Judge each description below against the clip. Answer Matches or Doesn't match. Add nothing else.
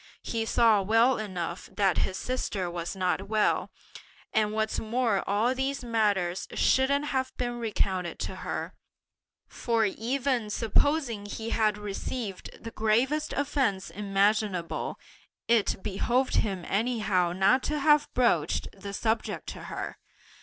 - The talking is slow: Matches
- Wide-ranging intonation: Doesn't match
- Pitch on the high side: Matches